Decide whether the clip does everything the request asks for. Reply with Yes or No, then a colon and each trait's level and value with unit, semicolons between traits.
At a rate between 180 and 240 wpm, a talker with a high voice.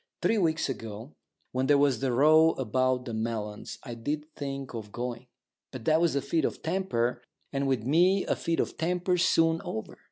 No: average, 190 wpm; low, 135 Hz